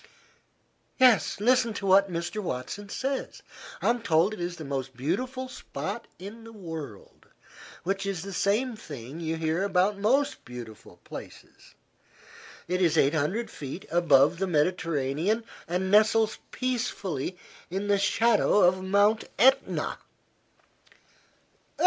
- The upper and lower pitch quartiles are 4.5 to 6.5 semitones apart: Yes, average, 5.2 semitones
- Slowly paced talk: Yes, slow, 125 wpm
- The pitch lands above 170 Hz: Yes, high, 190 Hz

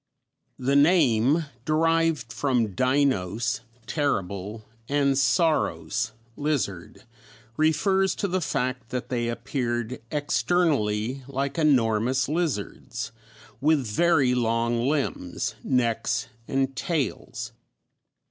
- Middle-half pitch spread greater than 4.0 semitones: Yes, average, 4.5 semitones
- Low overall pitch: Yes, low, 130 Hz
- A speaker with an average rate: No, slow, 90 wpm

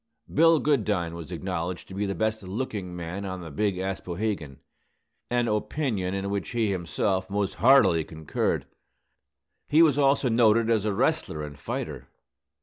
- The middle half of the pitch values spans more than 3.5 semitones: Yes, average, 4.4 semitones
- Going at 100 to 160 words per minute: Yes, average, 150 wpm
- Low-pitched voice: Yes, low, 100 Hz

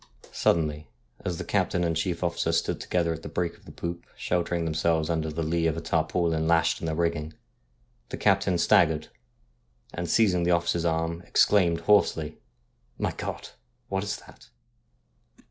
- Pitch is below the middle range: Yes, very low, 85 Hz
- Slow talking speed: No, average, 170 wpm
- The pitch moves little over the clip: Yes, narrow, 1.3 semitones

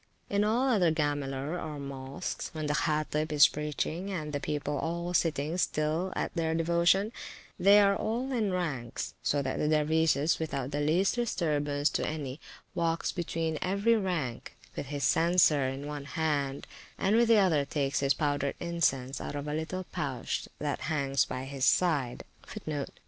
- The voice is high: No, medium, 155 Hz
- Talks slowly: No, average, 165 wpm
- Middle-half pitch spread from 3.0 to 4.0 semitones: Yes, average, 3.7 semitones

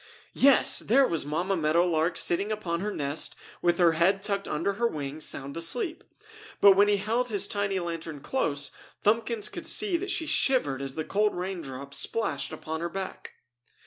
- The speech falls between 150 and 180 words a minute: Yes, average, 175 wpm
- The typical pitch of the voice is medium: Yes, medium, 180 Hz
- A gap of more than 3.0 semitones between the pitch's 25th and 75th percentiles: Yes, average, 5.0 semitones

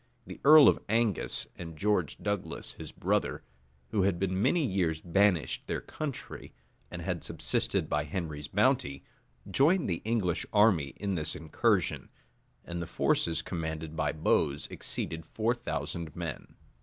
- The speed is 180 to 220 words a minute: No, average, 145 wpm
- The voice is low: Yes, very low, 90 Hz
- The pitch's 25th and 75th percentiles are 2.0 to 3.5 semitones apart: No, average, 4.7 semitones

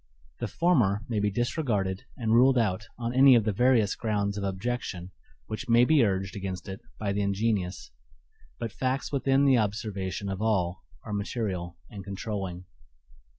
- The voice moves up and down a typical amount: Yes, average, 3.9 semitones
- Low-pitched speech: Yes, low, 105 Hz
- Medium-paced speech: Yes, average, 160 wpm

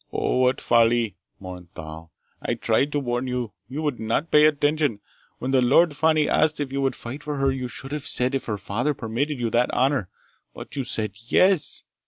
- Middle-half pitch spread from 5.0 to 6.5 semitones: No, average, 4.0 semitones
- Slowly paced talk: No, fast, 205 wpm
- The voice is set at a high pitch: No, low, 130 Hz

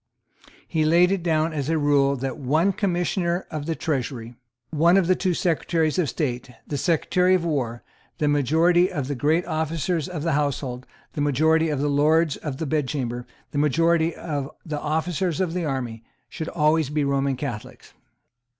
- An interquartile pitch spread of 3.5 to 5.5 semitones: No, average, 3.1 semitones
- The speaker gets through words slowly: No, average, 175 wpm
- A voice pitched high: No, medium, 155 Hz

